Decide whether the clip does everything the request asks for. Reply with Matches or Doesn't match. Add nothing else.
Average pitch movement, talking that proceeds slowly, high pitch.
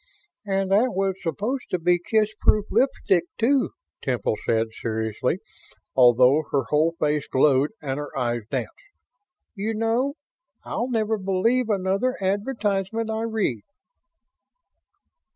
Doesn't match